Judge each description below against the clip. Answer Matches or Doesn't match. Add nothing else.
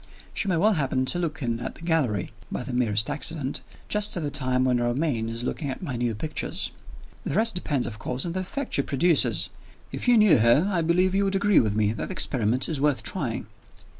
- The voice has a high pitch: Doesn't match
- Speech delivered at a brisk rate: Matches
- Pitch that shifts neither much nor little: Doesn't match